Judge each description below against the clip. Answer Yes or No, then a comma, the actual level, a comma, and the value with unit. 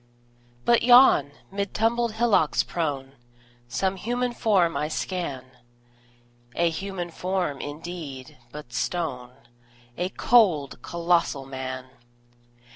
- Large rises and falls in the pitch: Yes, wide, 5.8 semitones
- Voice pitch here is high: No, medium, 170 Hz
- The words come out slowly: Yes, slow, 100 wpm